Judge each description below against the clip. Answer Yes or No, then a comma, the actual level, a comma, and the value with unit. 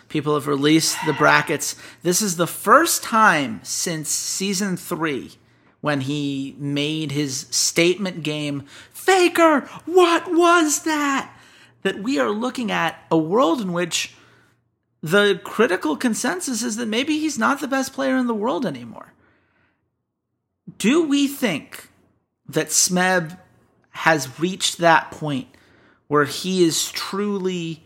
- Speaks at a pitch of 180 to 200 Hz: Yes, medium, 185 Hz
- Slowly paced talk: Yes, slow, 130 wpm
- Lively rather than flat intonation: Yes, wide, 8.4 semitones